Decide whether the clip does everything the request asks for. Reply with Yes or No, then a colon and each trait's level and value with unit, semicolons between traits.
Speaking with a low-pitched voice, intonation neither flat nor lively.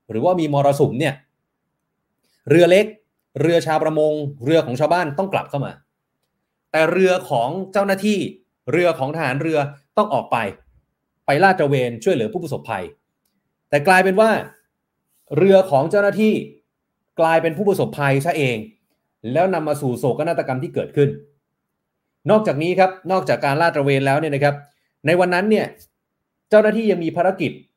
No: medium, 160 Hz; average, 4.6 semitones